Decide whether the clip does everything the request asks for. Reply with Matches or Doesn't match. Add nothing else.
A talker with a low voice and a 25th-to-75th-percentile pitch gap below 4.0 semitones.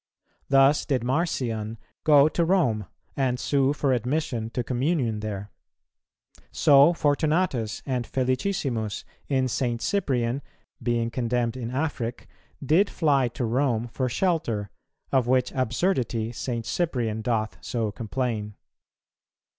Matches